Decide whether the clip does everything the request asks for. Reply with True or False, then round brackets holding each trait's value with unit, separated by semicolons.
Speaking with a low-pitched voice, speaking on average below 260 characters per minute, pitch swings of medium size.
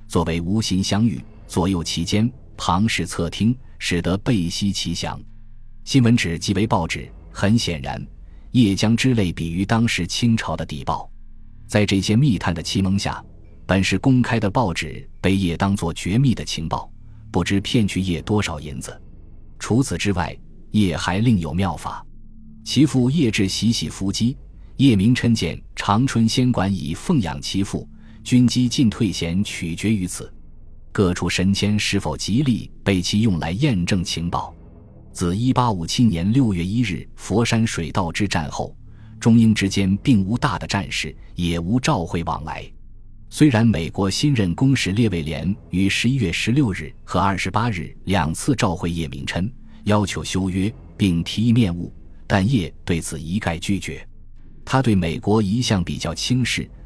True (100 Hz; 235 characters per minute; 4.9 semitones)